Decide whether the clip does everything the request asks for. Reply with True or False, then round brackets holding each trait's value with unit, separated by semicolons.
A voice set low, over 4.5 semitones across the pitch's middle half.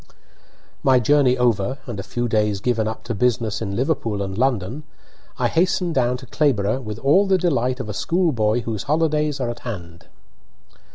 True (120 Hz; 4.9 semitones)